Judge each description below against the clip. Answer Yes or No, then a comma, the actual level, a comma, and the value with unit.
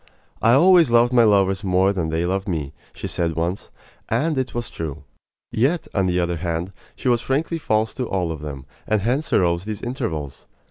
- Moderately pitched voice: No, very low, 95 Hz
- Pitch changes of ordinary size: No, wide, 6.0 semitones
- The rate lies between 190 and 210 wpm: Yes, average, 195 wpm